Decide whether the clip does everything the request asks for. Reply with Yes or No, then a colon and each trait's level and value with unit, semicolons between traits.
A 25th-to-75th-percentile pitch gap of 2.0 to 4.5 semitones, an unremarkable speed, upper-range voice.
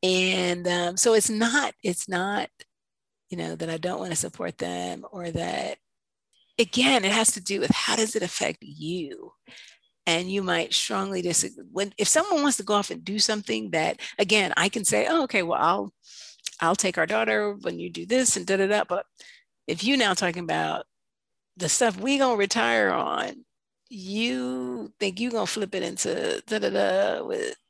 No: average, 4.9 semitones; average, 185 wpm; high, 200 Hz